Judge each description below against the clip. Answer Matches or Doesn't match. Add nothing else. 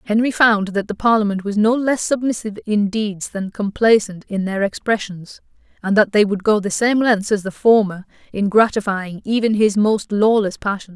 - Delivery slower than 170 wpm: Doesn't match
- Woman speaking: Matches